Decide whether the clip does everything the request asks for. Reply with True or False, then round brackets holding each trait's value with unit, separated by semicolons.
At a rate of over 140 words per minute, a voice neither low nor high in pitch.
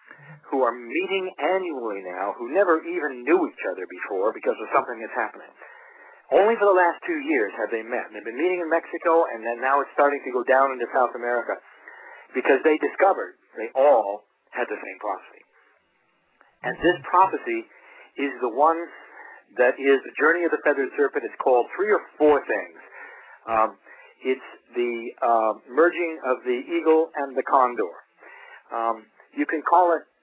True (175 wpm; 170 Hz)